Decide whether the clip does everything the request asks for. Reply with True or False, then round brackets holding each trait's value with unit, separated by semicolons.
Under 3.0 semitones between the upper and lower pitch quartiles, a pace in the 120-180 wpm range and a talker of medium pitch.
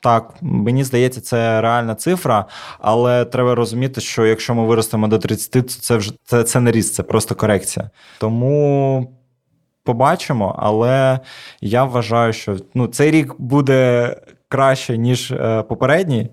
False (2.5 semitones; 140 wpm; 120 Hz)